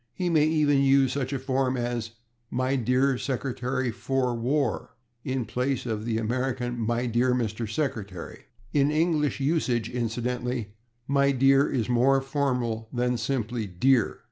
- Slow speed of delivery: No, average, 145 wpm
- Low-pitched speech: Yes, low, 125 Hz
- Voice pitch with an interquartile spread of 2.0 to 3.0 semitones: Yes, narrow, 2.4 semitones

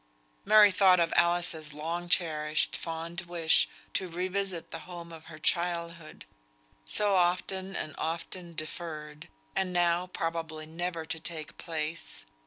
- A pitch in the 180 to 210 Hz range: No, medium, 170 Hz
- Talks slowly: Yes, slow, 130 wpm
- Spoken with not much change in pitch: Yes, narrow, 1.9 semitones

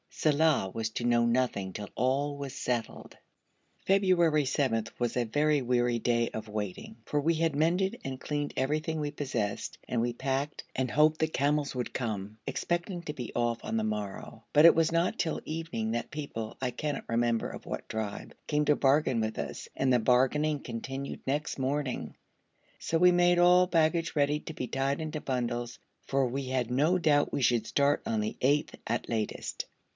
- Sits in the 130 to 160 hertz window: Yes, low, 135 Hz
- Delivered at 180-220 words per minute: Yes, average, 185 wpm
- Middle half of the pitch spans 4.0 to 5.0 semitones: Yes, average, 4.4 semitones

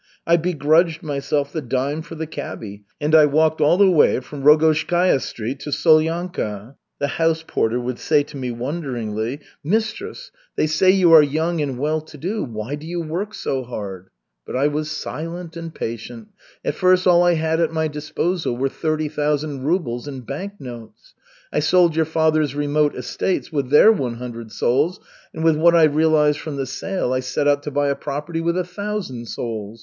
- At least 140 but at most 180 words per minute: No, average, 190 wpm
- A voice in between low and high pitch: Yes, medium, 150 Hz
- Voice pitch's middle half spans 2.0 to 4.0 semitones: Yes, average, 3.6 semitones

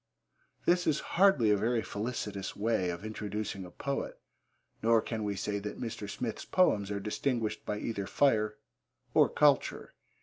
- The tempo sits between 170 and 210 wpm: No, average, 155 wpm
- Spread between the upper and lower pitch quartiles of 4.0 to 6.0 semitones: No, average, 3.0 semitones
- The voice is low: Yes, low, 110 Hz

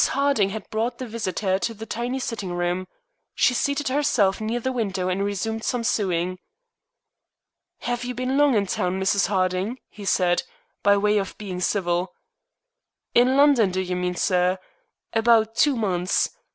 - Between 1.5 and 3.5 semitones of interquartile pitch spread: No, average, 4.5 semitones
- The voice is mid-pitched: No, high, 205 Hz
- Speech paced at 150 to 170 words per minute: Yes, average, 160 wpm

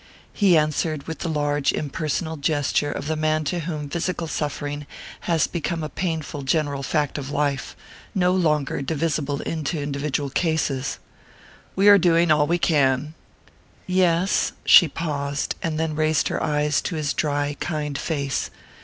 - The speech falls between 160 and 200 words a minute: No, average, 150 wpm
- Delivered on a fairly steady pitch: Yes, narrow, 2.3 semitones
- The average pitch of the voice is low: No, medium, 150 Hz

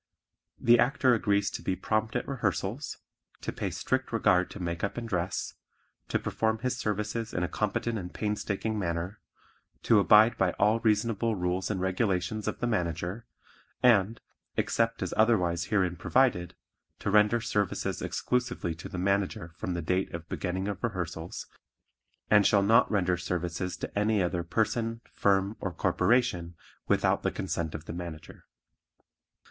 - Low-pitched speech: Yes, low, 100 Hz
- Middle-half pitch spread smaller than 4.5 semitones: Yes, average, 3.9 semitones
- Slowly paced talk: No, average, 155 wpm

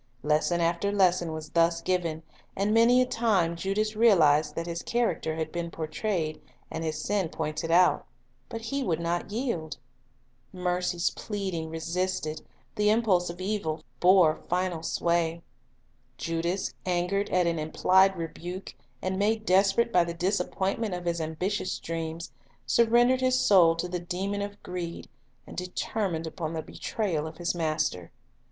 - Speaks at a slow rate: No, average, 145 wpm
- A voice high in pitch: No, medium, 175 Hz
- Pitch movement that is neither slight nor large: Yes, average, 3.3 semitones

